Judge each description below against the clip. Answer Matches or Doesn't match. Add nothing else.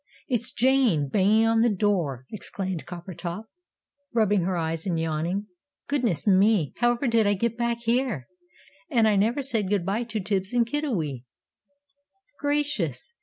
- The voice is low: Doesn't match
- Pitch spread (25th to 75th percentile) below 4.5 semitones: Doesn't match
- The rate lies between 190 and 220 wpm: Doesn't match